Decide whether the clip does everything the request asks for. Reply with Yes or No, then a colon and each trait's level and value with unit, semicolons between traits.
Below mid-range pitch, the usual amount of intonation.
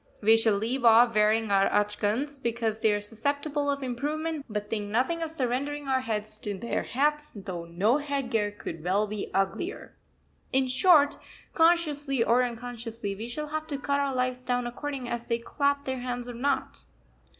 No: high, 245 Hz; average, 4.7 semitones